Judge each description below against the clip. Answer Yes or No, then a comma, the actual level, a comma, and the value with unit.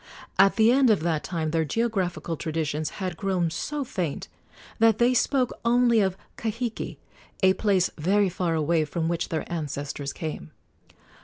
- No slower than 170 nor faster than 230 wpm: No, average, 155 wpm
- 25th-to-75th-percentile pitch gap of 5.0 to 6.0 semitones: Yes, wide, 5.6 semitones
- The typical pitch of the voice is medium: Yes, medium, 180 Hz